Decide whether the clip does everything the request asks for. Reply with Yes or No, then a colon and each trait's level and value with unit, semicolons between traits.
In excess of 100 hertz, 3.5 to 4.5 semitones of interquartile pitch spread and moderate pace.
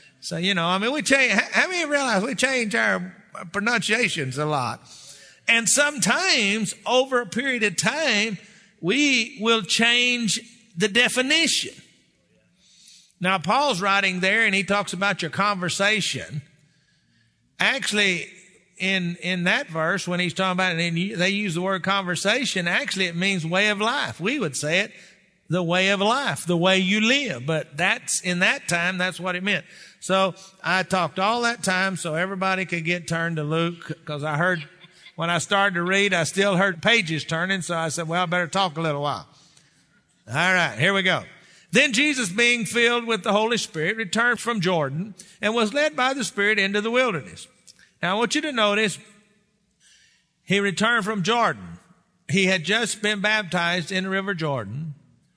Yes: high, 190 Hz; average, 3.8 semitones; average, 175 wpm